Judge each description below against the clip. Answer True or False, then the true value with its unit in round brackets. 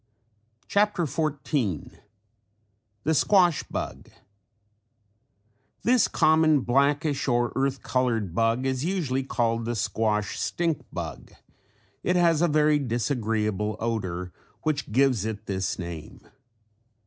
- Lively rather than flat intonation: True (5.7 semitones)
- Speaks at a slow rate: True (105 wpm)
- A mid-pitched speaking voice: False (130 Hz)